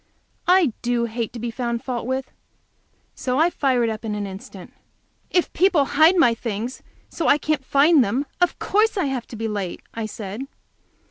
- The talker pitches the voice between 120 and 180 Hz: No, very high, 250 Hz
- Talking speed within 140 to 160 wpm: No, average, 190 wpm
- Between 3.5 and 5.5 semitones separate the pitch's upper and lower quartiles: Yes, average, 4.9 semitones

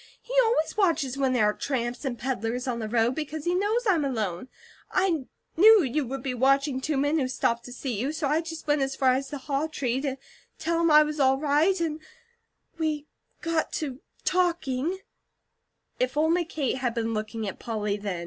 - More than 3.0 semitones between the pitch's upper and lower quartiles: Yes, average, 4.3 semitones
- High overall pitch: Yes, very high, 275 Hz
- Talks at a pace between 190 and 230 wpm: Yes, fast, 205 wpm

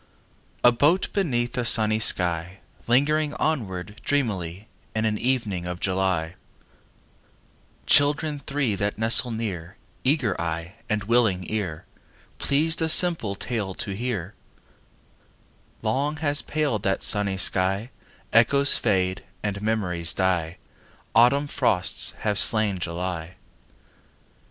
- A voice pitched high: No, low, 110 Hz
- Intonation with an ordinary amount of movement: No, wide, 5.8 semitones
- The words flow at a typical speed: No, slow, 115 wpm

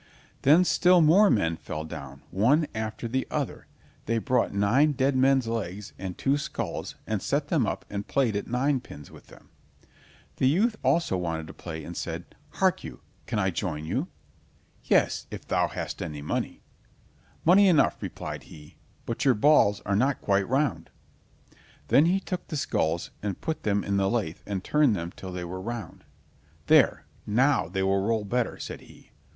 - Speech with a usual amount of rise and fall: No, wide, 6.9 semitones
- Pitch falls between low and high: No, low, 110 Hz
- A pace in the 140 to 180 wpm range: Yes, average, 175 wpm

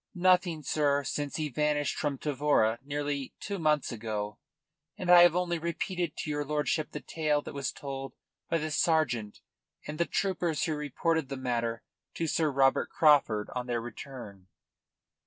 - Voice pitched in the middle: Yes, medium, 145 Hz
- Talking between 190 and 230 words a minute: No, average, 160 wpm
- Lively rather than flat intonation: No, average, 3.5 semitones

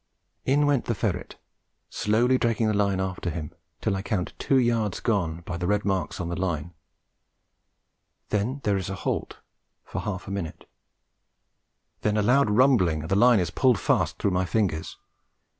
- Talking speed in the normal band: Yes, average, 175 wpm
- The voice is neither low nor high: No, low, 100 Hz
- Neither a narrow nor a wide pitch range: Yes, average, 4.2 semitones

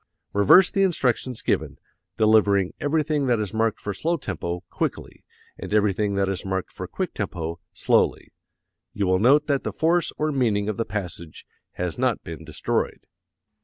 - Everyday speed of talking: Yes, average, 165 wpm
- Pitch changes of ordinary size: No, wide, 6.2 semitones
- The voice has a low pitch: Yes, low, 105 Hz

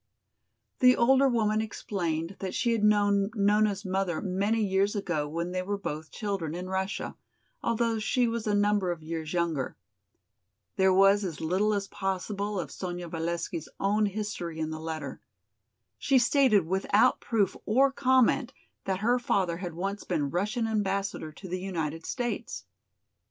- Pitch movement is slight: No, average, 3.7 semitones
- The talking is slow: No, average, 155 wpm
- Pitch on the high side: Yes, high, 195 Hz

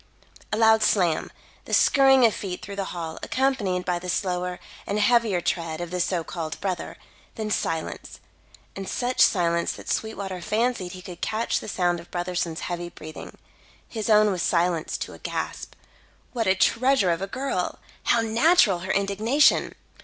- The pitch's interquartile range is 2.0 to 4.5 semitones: Yes, average, 4.0 semitones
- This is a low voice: No, high, 190 Hz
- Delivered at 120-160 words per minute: No, average, 170 wpm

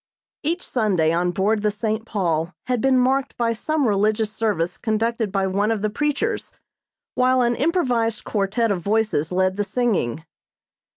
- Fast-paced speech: No, average, 160 wpm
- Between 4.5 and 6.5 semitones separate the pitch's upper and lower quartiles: No, average, 3.8 semitones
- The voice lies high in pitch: Yes, high, 215 Hz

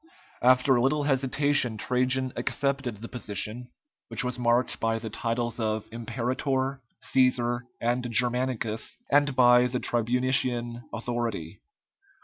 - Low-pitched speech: Yes, low, 125 Hz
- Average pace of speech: No, slow, 120 wpm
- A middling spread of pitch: No, narrow, 1.8 semitones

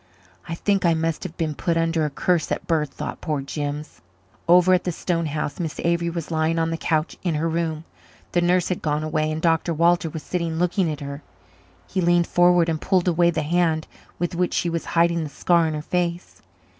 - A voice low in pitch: No, medium, 165 Hz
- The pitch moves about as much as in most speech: No, narrow, 1.9 semitones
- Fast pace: Yes, fast, 220 wpm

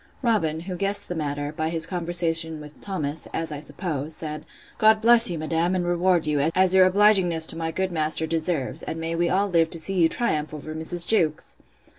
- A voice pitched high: No, medium, 165 Hz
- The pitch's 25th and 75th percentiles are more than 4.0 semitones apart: No, average, 2.9 semitones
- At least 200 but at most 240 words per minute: Yes, fast, 205 wpm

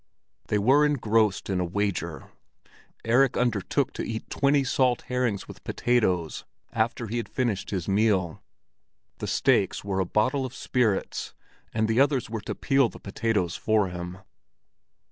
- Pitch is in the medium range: No, low, 110 Hz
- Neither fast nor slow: Yes, average, 150 wpm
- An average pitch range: Yes, average, 4.4 semitones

